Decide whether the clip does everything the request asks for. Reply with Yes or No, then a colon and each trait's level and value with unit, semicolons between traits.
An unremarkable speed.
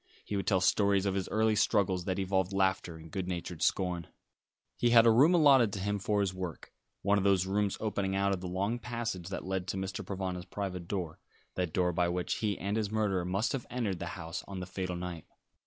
No: fast, 225 wpm